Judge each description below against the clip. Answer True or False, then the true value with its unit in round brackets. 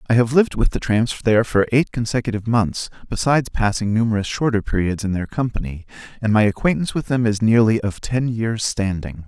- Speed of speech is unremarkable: True (195 wpm)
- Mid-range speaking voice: False (110 Hz)